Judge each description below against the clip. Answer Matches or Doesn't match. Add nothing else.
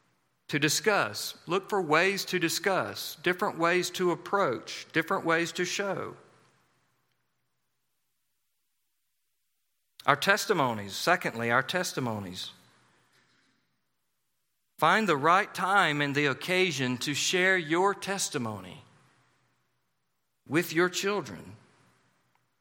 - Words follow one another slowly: Matches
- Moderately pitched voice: Matches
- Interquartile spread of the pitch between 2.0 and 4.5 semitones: Doesn't match